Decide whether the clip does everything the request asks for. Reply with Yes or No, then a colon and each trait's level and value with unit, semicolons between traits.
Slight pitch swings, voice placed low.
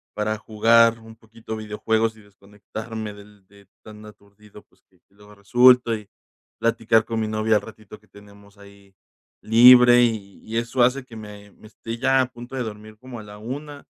Yes: narrow, 1.9 semitones; low, 110 Hz